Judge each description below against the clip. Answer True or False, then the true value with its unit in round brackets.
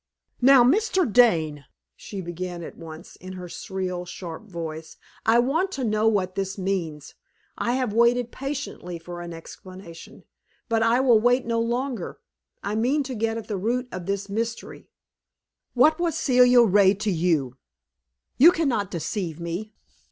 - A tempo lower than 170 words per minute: True (160 wpm)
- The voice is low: False (210 Hz)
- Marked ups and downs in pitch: True (5.7 semitones)